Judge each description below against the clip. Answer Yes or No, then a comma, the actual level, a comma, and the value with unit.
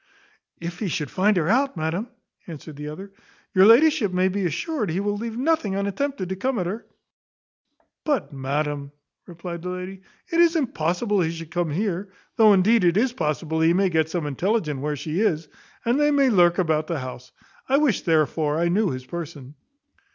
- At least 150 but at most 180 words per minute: No, average, 190 wpm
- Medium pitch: Yes, medium, 180 Hz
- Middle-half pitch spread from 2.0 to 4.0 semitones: No, average, 5.3 semitones